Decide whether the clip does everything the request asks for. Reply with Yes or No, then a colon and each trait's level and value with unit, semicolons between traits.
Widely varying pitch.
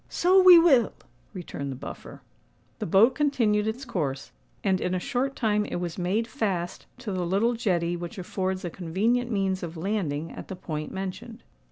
No: average, 4.8 semitones